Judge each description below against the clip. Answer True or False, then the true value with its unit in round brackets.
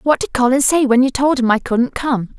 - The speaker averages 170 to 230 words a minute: False (275 wpm)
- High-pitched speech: True (255 Hz)